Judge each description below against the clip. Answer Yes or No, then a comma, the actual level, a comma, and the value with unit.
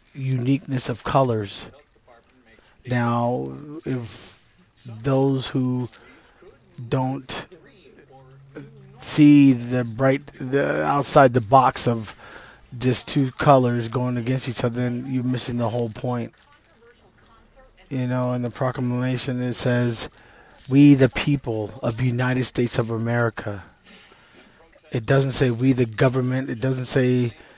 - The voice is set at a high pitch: No, low, 125 Hz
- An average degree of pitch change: No, narrow, 1.8 semitones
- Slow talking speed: Yes, slow, 115 wpm